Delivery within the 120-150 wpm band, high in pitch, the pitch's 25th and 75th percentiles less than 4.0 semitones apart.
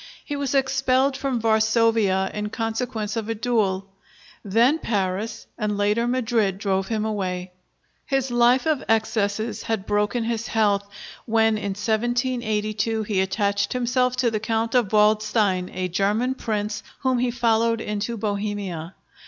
Yes: average, 140 wpm; high, 220 Hz; average, 2.7 semitones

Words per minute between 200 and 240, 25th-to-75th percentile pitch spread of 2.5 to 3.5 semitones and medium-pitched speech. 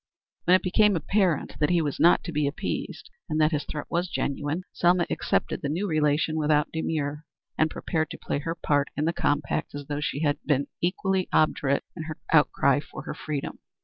Yes: fast, 205 wpm; average, 2.8 semitones; medium, 155 Hz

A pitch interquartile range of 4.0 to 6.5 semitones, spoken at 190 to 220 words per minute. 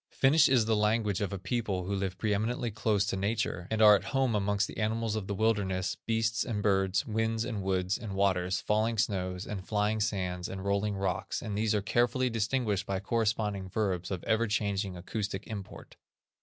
No: narrow, 2.5 semitones; average, 195 wpm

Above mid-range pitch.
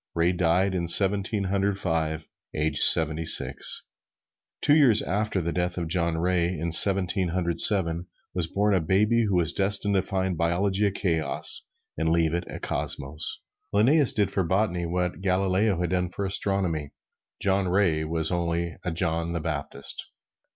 No: very low, 90 Hz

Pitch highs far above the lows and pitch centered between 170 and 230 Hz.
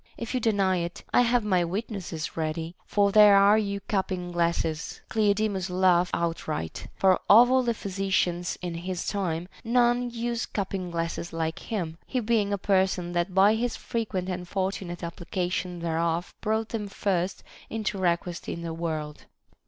No: average, 3.5 semitones; medium, 185 Hz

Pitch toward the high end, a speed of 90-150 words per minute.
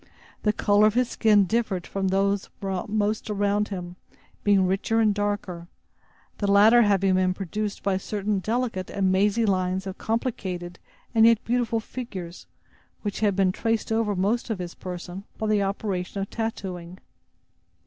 No: high, 200 Hz; average, 160 wpm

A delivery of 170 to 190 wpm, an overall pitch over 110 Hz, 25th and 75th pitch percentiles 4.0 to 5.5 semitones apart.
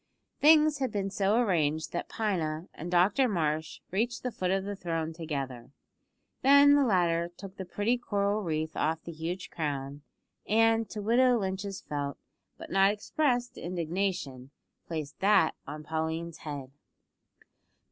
No: average, 145 wpm; medium, 185 Hz; average, 5.1 semitones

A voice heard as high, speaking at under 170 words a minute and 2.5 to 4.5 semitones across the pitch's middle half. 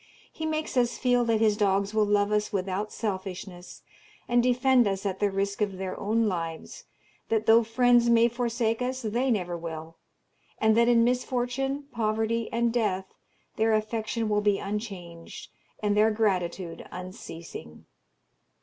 Yes: high, 215 Hz; average, 150 wpm; average, 3.4 semitones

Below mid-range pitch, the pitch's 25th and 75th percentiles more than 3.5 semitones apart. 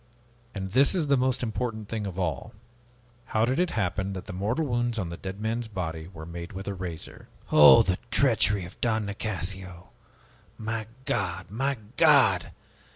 Yes: low, 105 Hz; average, 4.5 semitones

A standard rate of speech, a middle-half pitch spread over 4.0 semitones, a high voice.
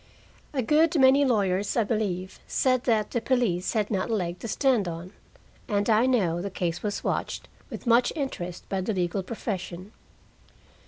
Yes: average, 170 wpm; average, 5.0 semitones; high, 210 Hz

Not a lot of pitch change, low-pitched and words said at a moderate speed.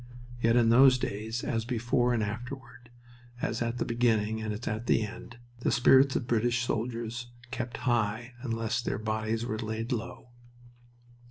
Yes: narrow, 1.6 semitones; low, 115 Hz; average, 160 wpm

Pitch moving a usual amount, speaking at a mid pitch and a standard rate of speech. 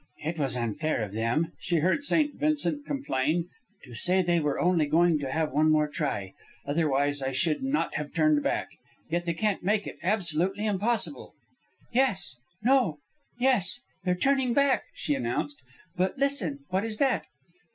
No: wide, 6.9 semitones; medium, 170 Hz; average, 160 wpm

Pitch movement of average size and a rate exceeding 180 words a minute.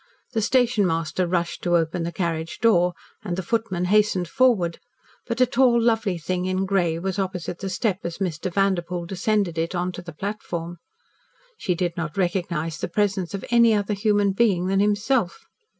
No: average, 3.2 semitones; average, 170 wpm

